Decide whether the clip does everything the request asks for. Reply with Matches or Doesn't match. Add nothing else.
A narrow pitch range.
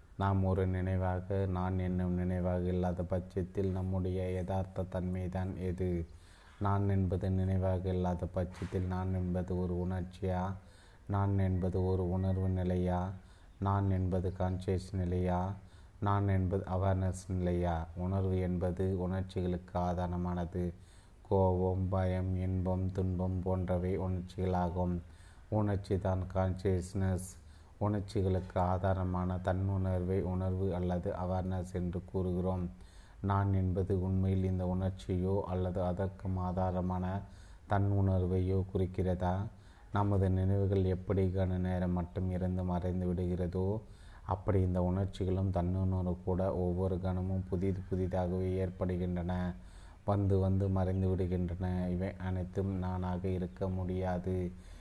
Matches